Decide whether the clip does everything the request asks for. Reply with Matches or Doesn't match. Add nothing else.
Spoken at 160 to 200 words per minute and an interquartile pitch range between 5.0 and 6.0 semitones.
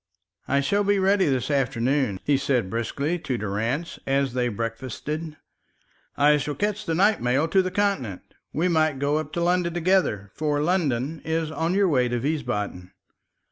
Matches